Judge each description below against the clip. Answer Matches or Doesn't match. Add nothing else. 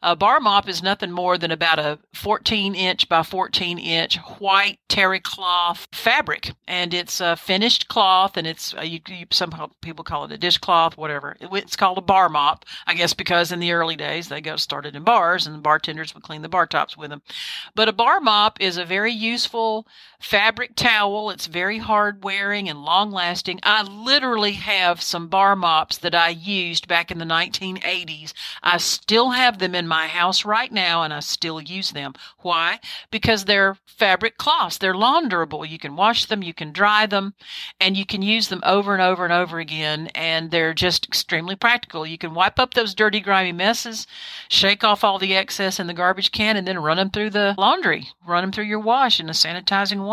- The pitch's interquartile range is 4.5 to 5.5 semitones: Doesn't match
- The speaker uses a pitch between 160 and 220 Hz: Matches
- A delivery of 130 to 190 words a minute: Doesn't match